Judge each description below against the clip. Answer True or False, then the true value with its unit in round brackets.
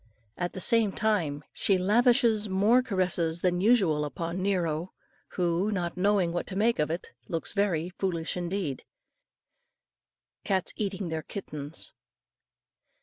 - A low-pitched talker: False (185 Hz)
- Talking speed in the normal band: False (130 wpm)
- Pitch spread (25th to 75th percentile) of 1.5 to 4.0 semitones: True (3.4 semitones)